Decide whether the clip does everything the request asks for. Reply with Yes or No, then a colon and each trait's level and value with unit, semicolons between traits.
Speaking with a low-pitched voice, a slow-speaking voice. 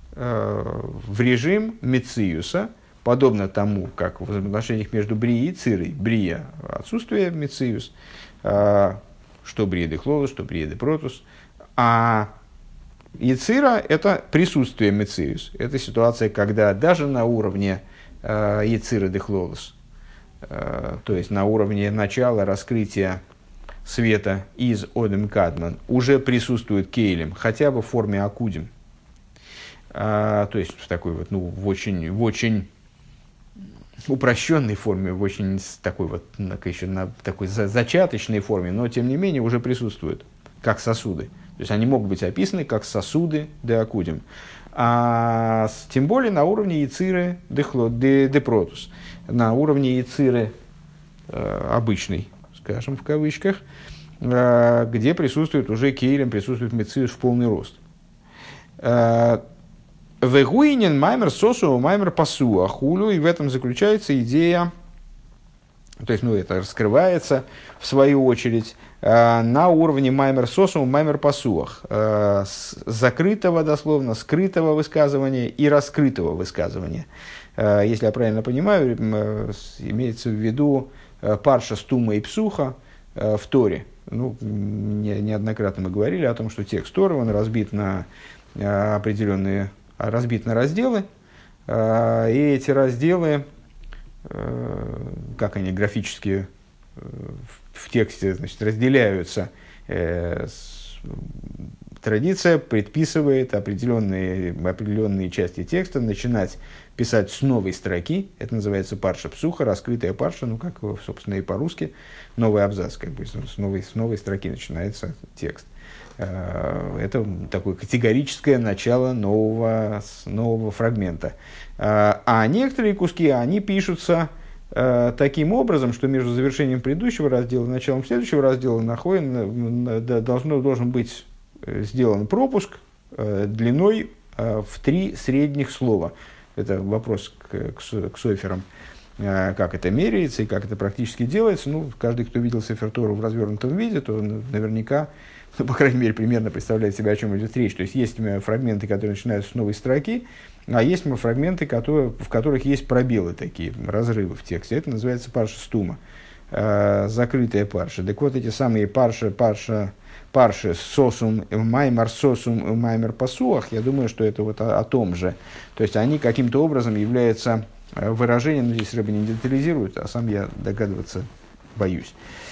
No: low, 115 Hz; average, 125 wpm